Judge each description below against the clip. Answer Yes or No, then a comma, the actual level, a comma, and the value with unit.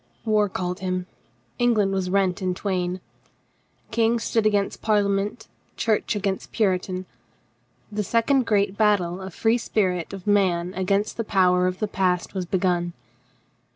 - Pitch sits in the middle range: No, high, 195 Hz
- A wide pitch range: No, narrow, 2.6 semitones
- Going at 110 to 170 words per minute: Yes, average, 155 wpm